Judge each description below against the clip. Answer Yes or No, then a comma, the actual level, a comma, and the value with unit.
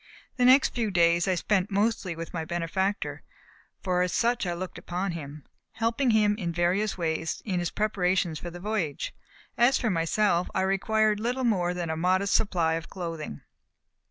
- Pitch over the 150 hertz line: Yes, medium, 185 Hz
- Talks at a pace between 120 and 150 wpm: No, average, 175 wpm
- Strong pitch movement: No, average, 4.0 semitones